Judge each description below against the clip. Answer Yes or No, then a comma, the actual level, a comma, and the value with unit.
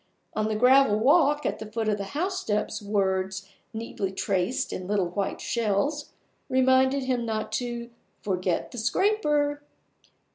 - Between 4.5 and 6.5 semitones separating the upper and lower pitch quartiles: Yes, average, 4.8 semitones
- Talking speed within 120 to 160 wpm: Yes, average, 140 wpm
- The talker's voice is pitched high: Yes, high, 225 Hz